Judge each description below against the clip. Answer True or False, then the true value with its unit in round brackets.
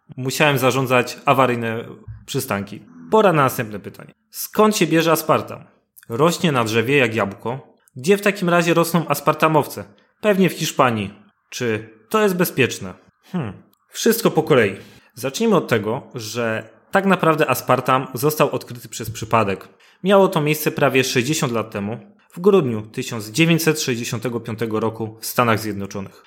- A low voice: True (130 Hz)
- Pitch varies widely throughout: True (6.4 semitones)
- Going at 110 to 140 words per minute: True (135 wpm)